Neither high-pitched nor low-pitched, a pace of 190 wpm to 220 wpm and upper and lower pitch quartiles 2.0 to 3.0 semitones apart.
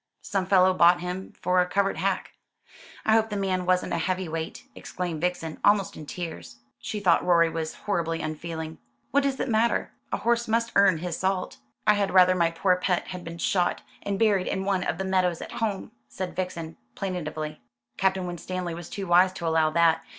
Yes: medium, 180 Hz; average, 195 wpm; narrow, 2.6 semitones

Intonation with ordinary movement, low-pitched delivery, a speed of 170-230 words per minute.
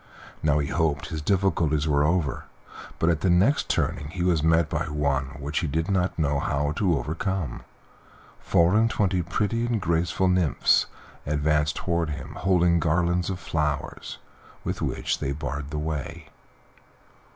No: average, 3.3 semitones; very low, 80 Hz; average, 155 wpm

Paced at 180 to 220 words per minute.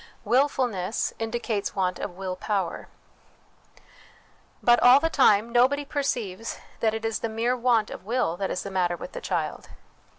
No: average, 160 wpm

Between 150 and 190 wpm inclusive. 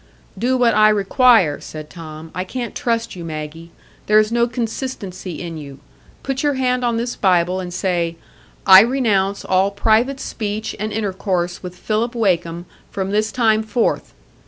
Yes: average, 160 wpm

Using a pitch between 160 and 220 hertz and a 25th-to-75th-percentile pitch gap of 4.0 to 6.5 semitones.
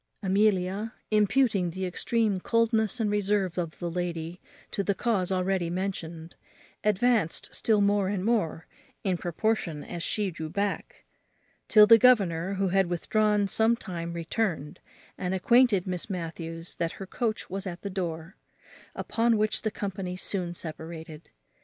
No: high, 190 Hz; average, 3.5 semitones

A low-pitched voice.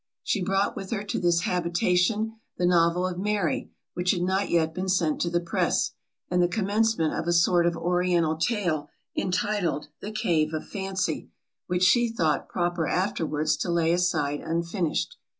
No: medium, 180 Hz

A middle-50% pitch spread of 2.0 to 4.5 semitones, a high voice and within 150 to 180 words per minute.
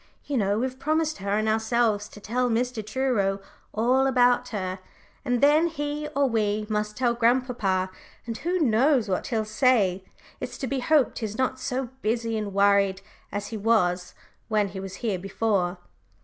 Yes: average, 4.1 semitones; high, 225 Hz; average, 170 wpm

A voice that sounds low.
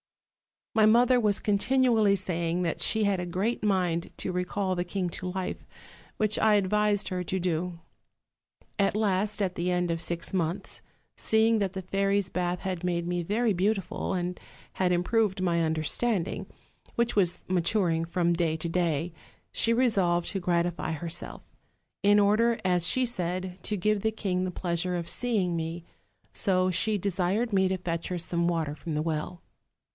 No: medium, 185 Hz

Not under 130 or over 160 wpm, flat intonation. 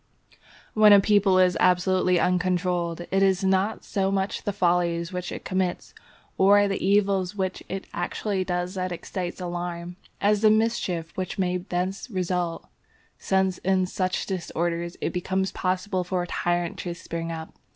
Yes: average, 155 wpm; narrow, 1.6 semitones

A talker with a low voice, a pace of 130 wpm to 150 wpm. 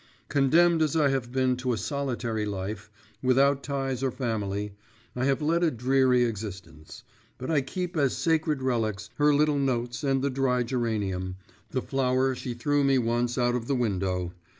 No: low, 130 Hz; average, 175 wpm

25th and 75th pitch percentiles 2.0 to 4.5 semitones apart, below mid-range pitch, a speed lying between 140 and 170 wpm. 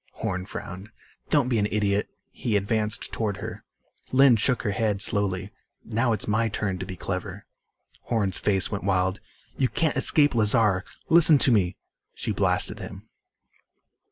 Yes: average, 2.8 semitones; low, 105 Hz; average, 155 wpm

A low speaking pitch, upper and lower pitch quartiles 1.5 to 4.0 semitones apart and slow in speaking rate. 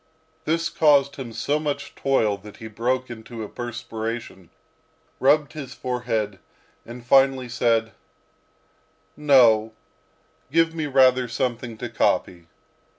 Yes: low, 125 Hz; average, 3.5 semitones; slow, 115 wpm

